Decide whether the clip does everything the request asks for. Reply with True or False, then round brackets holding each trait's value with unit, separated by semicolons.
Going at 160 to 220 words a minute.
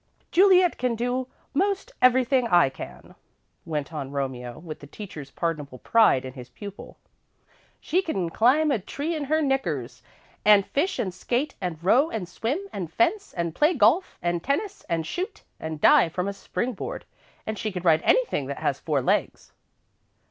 True (170 wpm)